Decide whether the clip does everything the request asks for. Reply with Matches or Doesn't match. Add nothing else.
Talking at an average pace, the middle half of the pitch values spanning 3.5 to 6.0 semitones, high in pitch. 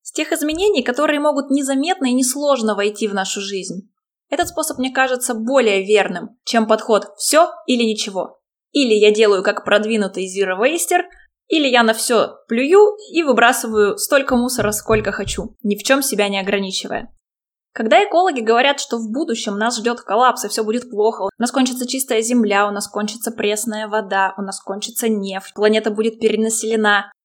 Doesn't match